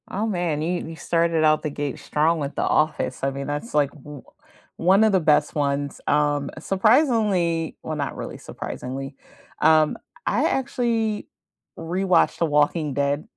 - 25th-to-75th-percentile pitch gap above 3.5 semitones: Yes, average, 4.2 semitones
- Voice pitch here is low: No, medium, 155 Hz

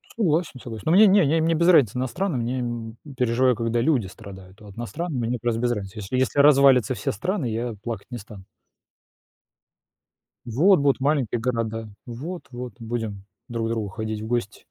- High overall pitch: No, low, 120 Hz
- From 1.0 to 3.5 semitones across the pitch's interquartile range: No, average, 4.0 semitones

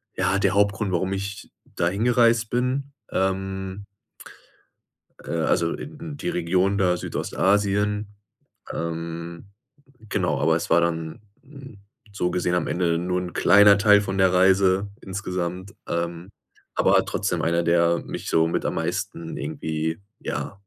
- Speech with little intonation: No, average, 3.1 semitones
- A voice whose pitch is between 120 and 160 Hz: No, very low, 95 Hz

